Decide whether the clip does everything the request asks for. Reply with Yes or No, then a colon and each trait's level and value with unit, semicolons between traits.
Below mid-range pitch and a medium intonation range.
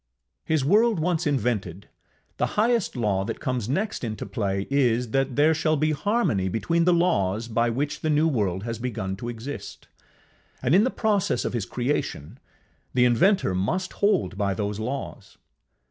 No: low, 125 Hz; wide, 7.4 semitones